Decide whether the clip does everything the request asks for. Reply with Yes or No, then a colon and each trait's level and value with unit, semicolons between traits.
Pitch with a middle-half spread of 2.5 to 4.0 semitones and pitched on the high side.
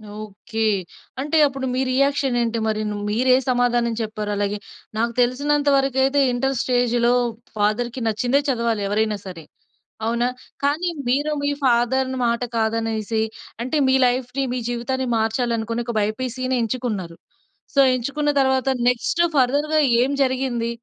Yes: average, 2.8 semitones; high, 245 Hz